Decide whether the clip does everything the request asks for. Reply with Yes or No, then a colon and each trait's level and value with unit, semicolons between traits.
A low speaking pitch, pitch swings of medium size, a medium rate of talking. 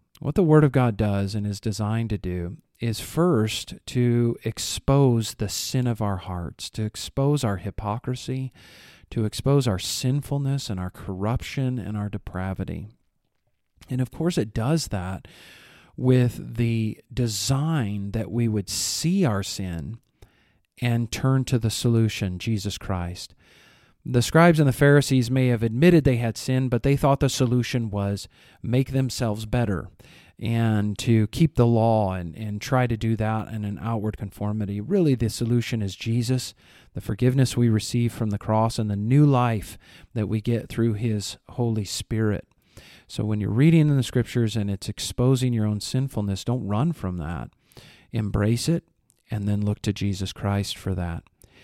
Yes: low, 115 Hz; average, 3.8 semitones; average, 165 wpm